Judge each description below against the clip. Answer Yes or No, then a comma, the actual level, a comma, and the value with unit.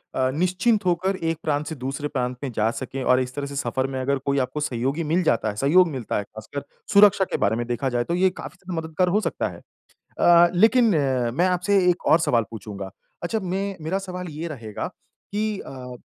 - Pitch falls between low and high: Yes, medium, 145 Hz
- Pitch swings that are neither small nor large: No, wide, 6.2 semitones